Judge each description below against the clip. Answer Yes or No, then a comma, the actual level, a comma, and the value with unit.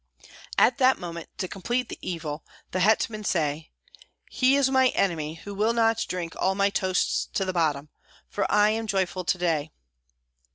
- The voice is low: No, high, 190 Hz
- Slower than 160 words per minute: No, average, 170 wpm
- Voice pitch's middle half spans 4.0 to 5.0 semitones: Yes, average, 4.7 semitones